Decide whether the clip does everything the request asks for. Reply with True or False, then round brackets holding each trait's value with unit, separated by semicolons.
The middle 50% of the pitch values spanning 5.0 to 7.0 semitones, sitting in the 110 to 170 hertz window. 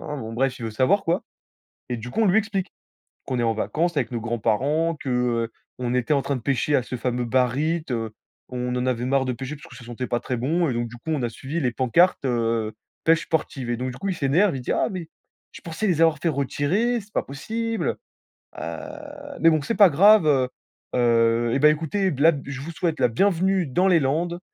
True (5.6 semitones; 140 Hz)